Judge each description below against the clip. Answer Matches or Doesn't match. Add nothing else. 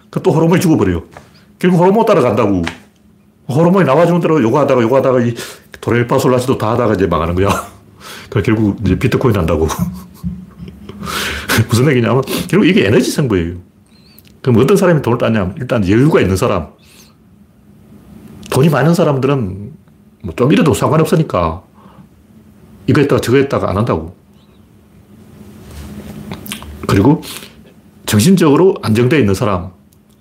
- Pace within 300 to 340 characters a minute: Matches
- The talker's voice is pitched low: Matches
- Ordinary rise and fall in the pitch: Doesn't match